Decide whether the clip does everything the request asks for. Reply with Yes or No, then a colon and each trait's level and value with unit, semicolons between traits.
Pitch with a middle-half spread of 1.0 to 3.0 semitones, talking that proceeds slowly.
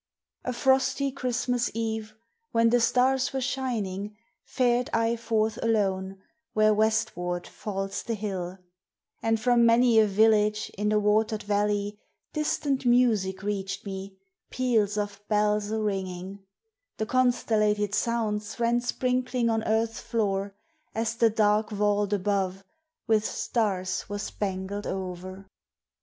Yes: narrow, 2.6 semitones; slow, 125 wpm